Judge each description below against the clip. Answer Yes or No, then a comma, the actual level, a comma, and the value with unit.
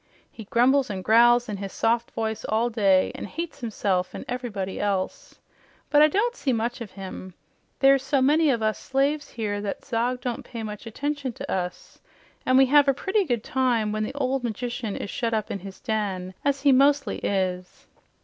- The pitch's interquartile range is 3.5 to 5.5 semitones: Yes, average, 4.6 semitones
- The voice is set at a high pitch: Yes, high, 235 Hz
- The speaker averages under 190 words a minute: No, average, 195 wpm